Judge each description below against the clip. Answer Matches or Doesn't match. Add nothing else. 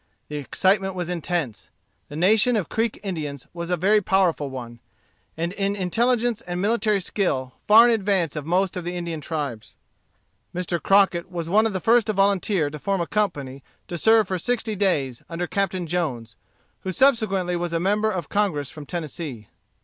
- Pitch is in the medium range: Matches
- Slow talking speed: Doesn't match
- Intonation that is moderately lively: Matches